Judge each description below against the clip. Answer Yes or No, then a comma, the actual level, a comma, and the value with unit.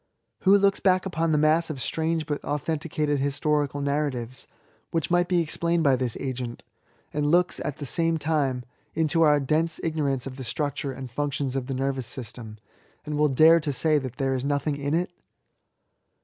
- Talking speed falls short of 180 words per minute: No, average, 185 wpm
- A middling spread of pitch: Yes, average, 3.2 semitones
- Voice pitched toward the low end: No, medium, 145 Hz